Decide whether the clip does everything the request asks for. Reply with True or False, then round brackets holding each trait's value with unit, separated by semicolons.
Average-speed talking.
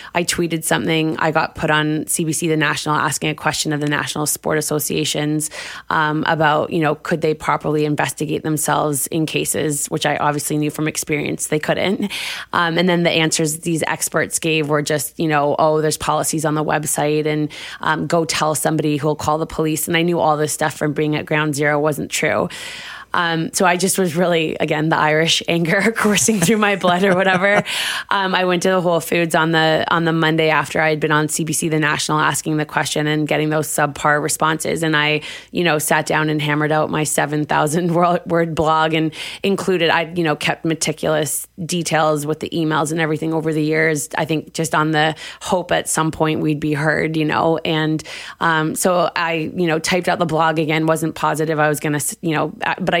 False (210 wpm)